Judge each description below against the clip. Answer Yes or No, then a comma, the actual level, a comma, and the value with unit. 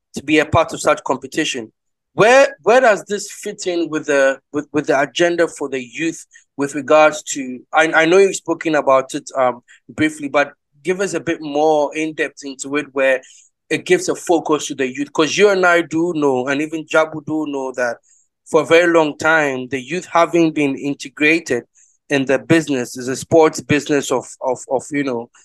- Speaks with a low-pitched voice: No, medium, 155 Hz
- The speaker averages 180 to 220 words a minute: Yes, fast, 205 wpm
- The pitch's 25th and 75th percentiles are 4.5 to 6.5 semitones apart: No, average, 2.8 semitones